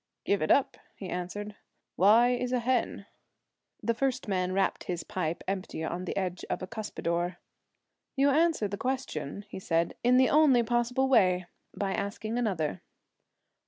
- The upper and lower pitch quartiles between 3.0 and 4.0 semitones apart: No, average, 5.3 semitones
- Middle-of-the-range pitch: No, high, 205 Hz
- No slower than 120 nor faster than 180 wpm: Yes, average, 160 wpm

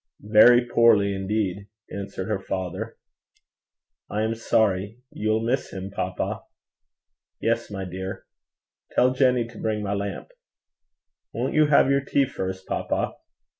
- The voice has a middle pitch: No, low, 105 Hz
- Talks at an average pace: No, slow, 130 wpm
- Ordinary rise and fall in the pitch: Yes, average, 3.2 semitones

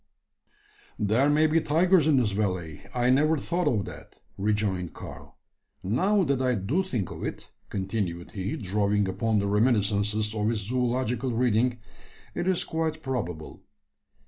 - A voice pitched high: No, low, 115 Hz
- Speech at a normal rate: Yes, average, 145 wpm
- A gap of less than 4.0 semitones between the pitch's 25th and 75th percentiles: No, wide, 5.5 semitones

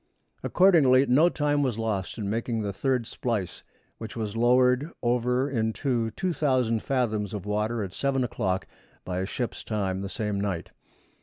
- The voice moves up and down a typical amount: Yes, average, 3.8 semitones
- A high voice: No, low, 115 Hz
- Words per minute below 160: Yes, average, 150 wpm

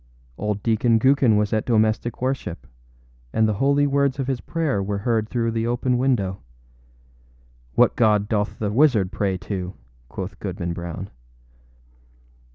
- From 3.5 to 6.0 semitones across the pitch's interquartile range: Yes, average, 4.0 semitones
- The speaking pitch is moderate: No, low, 110 Hz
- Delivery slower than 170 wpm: Yes, average, 145 wpm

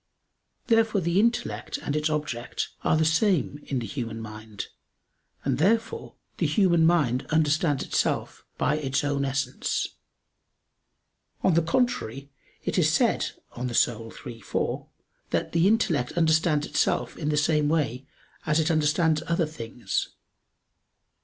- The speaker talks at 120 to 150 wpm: Yes, slow, 135 wpm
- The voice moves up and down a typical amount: Yes, average, 4.3 semitones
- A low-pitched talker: No, medium, 150 Hz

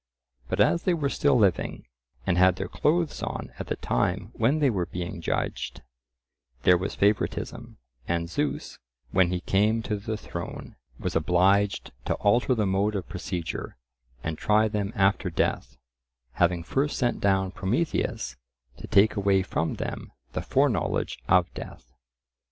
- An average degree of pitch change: Yes, average, 3.6 semitones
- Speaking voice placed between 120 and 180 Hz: No, low, 100 Hz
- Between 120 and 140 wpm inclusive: No, average, 150 wpm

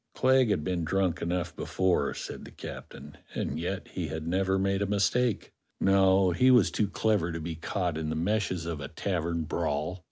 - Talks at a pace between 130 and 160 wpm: No, average, 190 wpm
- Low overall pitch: Yes, very low, 90 Hz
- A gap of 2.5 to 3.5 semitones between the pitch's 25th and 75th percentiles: Yes, average, 3.0 semitones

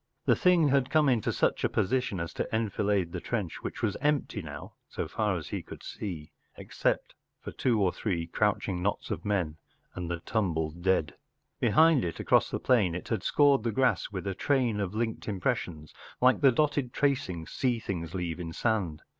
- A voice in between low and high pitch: No, low, 105 Hz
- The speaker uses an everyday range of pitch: No, wide, 6.3 semitones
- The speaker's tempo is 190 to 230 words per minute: Yes, average, 195 wpm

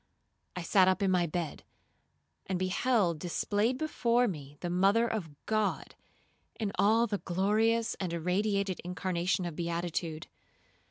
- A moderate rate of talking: No, slow, 130 wpm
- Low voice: No, medium, 185 Hz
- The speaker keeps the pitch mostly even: No, average, 3.8 semitones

